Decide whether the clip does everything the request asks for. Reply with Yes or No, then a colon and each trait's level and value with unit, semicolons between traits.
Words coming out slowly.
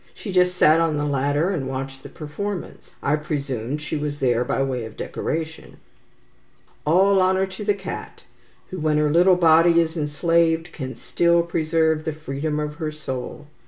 No: average, 170 wpm